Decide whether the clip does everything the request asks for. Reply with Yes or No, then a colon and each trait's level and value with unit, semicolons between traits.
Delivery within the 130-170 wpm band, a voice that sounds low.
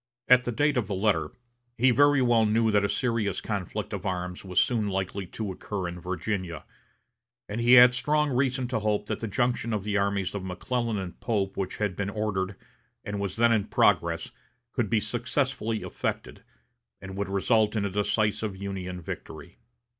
No: average, 185 wpm; low, 105 Hz